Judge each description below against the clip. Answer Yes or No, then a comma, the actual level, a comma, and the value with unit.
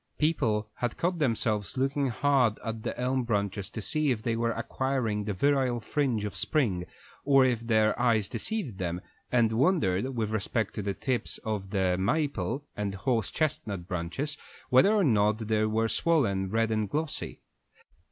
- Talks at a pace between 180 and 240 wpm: No, average, 160 wpm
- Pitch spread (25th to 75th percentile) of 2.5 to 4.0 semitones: No, average, 4.5 semitones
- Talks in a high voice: No, low, 115 Hz